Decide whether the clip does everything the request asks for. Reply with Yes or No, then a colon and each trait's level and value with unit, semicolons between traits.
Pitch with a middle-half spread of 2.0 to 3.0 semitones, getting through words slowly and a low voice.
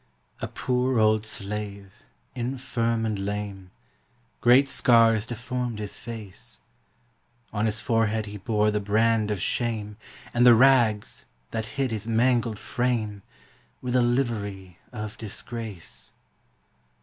Yes: narrow, 2.5 semitones; slow, 120 wpm; low, 110 Hz